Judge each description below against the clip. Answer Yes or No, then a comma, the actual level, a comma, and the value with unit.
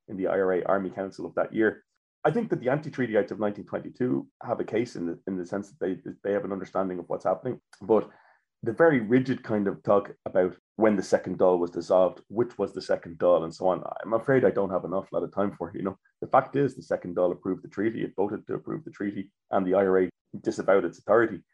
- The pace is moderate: No, fast, 250 wpm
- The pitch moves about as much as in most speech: Yes, average, 4.7 semitones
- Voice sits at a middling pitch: No, low, 100 Hz